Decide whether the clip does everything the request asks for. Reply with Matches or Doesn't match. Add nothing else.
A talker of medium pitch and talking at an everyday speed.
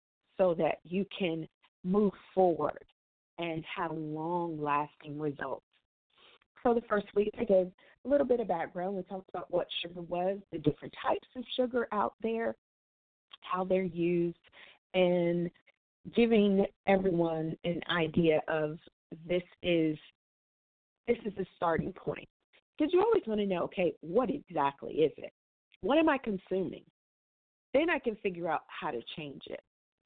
Matches